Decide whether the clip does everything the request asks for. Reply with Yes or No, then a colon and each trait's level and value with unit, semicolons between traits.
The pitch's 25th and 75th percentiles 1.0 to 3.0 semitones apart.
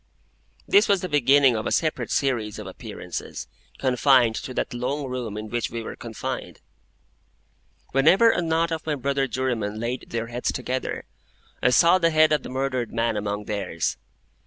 No: average, 4.5 semitones